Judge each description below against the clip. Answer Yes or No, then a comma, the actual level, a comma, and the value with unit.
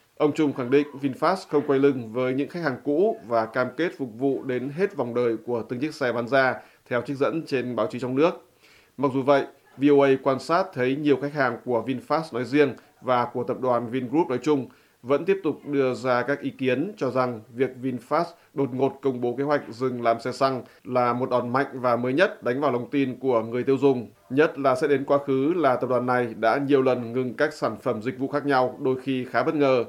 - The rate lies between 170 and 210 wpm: No, average, 240 wpm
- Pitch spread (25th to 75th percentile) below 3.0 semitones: Yes, narrow, 2.4 semitones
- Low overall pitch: Yes, low, 130 Hz